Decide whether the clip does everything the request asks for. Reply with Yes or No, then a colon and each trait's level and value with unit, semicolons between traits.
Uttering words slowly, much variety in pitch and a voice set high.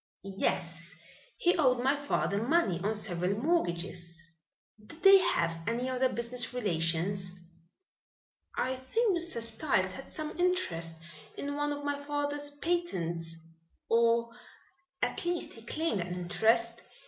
Yes: slow, 125 wpm; wide, 8.1 semitones; high, 235 Hz